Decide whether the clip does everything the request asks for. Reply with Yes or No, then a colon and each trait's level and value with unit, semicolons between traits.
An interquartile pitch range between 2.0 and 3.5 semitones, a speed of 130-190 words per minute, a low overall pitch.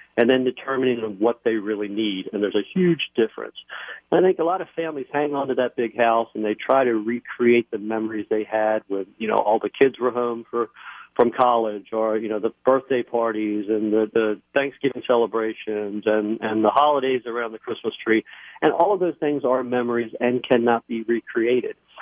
No: average, 3.0 semitones; average, 200 wpm; low, 120 Hz